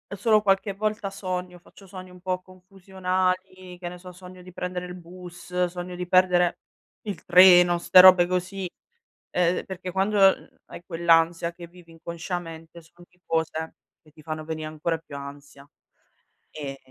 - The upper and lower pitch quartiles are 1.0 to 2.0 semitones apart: Yes, narrow, 1.6 semitones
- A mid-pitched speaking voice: Yes, medium, 180 Hz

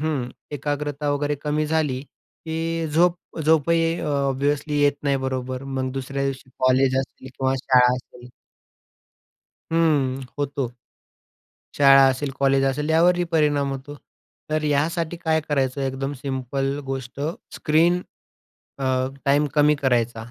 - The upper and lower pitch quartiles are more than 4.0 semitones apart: No, narrow, 2.4 semitones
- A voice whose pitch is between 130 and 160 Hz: Yes, medium, 140 Hz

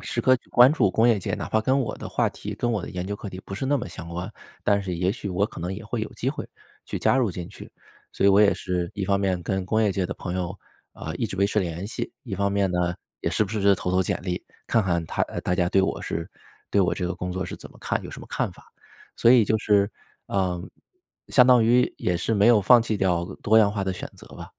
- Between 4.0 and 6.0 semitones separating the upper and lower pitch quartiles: No, average, 3.3 semitones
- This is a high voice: No, low, 100 Hz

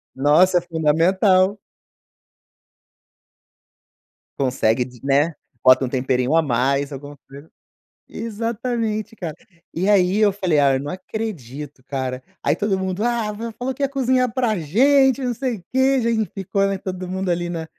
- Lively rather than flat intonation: Yes, wide, 7.7 semitones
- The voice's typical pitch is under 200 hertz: Yes, medium, 185 Hz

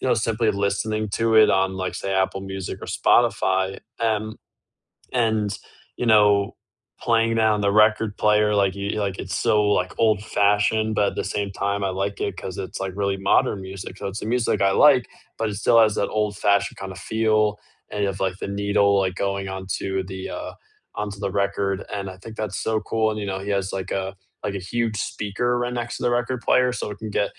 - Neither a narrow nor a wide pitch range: No, narrow, 2.0 semitones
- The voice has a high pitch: No, low, 100 Hz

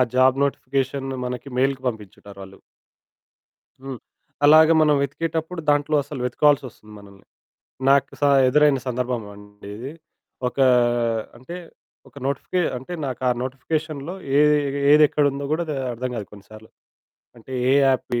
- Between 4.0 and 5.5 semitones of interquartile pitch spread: No, average, 3.6 semitones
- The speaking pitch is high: No, low, 135 Hz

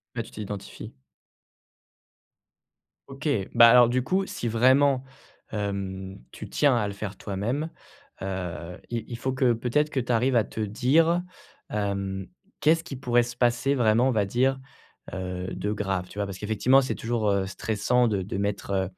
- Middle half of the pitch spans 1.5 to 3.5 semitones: No, average, 4.4 semitones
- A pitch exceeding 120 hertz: No, low, 115 Hz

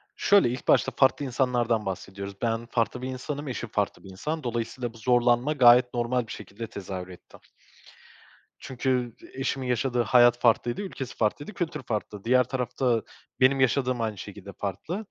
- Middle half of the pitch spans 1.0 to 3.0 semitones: Yes, narrow, 2.5 semitones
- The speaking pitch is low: Yes, low, 120 Hz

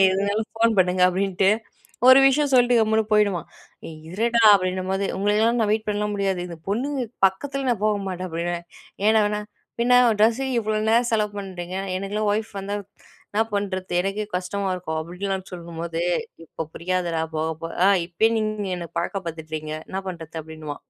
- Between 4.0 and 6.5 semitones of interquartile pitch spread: No, average, 3.5 semitones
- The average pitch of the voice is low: No, high, 195 Hz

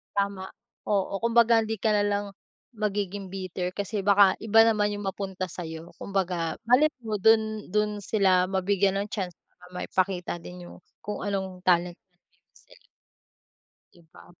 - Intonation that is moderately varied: No, narrow, 2.3 semitones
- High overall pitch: Yes, high, 200 Hz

